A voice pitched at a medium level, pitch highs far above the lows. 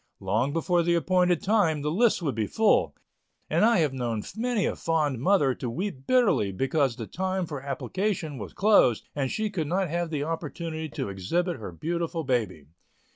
Yes: medium, 160 Hz; wide, 6.0 semitones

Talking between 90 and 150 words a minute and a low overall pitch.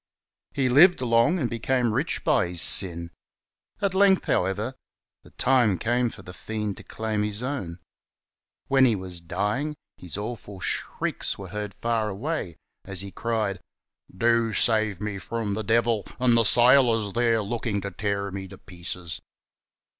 No: average, 160 wpm; low, 110 Hz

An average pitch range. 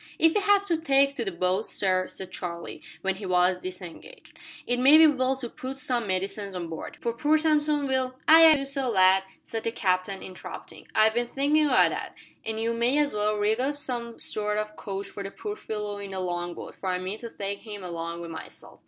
No: wide, 6.4 semitones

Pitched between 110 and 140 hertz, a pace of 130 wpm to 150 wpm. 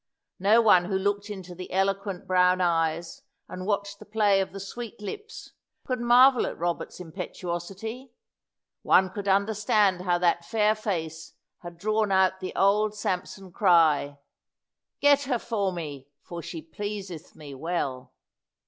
No: high, 190 Hz; average, 145 wpm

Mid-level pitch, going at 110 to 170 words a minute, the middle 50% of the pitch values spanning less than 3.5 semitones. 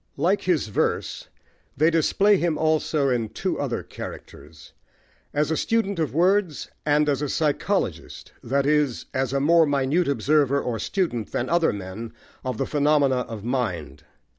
No: medium, 145 Hz; average, 155 wpm; average, 4.7 semitones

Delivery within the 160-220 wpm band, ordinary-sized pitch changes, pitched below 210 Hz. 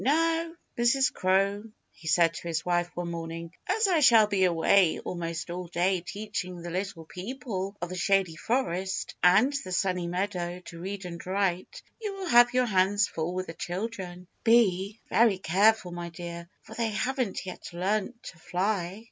Yes: average, 175 wpm; average, 3.9 semitones; medium, 185 Hz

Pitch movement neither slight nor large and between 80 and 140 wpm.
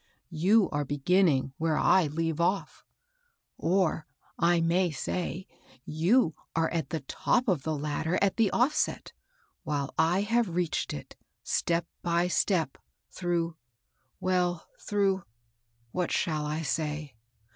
Yes: average, 3.4 semitones; slow, 135 wpm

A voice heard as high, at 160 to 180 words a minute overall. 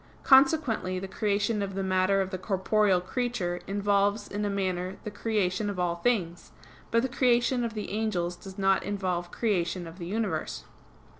Yes: high, 200 Hz; average, 170 wpm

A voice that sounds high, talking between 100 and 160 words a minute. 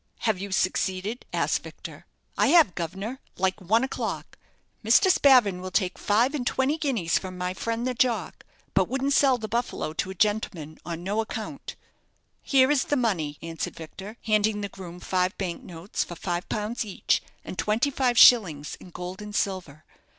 No: high, 205 Hz; average, 175 wpm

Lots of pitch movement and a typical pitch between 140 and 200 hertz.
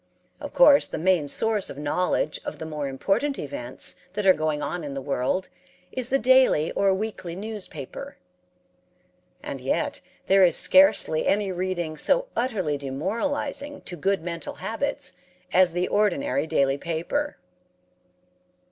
Yes: wide, 6.4 semitones; medium, 185 Hz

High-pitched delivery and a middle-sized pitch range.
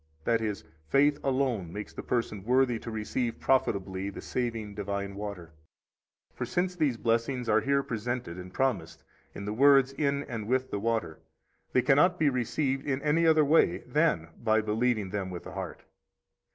No: low, 120 Hz; average, 4.8 semitones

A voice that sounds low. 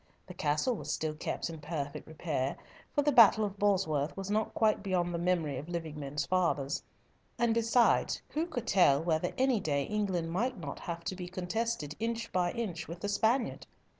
No: medium, 180 Hz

